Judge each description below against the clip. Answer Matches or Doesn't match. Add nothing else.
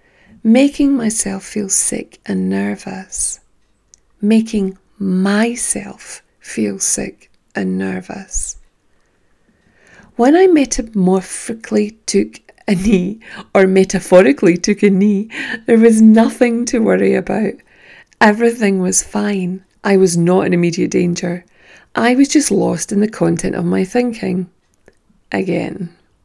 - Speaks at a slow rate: Matches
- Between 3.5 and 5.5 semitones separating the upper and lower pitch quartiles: Matches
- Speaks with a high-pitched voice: Matches